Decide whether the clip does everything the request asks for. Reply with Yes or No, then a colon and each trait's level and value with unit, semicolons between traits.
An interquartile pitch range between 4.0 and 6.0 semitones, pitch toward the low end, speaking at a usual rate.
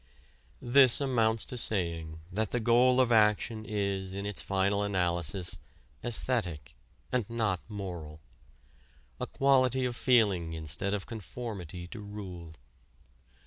No: average, 4.9 semitones; low, 105 Hz; slow, 120 wpm